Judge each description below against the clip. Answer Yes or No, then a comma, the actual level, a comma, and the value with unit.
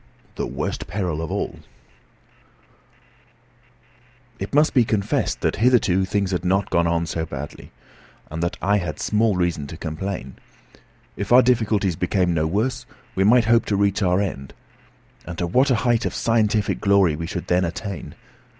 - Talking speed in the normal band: Yes, average, 165 wpm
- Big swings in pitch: No, average, 4.1 semitones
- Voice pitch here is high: No, very low, 95 Hz